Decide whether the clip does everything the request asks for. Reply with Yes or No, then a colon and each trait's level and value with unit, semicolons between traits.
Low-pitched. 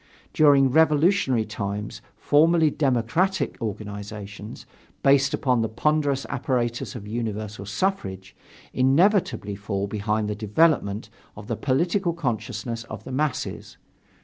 Yes: low, 120 Hz